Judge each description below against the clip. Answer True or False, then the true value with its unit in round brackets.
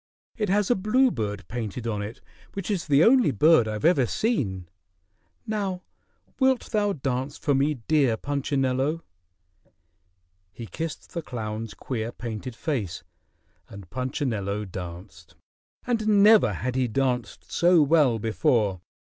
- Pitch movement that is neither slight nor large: False (7.6 semitones)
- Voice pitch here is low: True (130 Hz)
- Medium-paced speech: False (130 wpm)